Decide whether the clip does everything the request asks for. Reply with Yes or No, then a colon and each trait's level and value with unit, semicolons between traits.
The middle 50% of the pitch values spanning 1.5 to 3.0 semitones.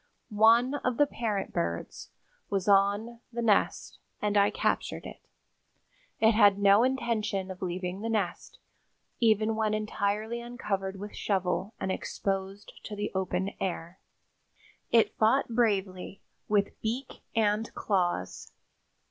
Yes: average, 2.7 semitones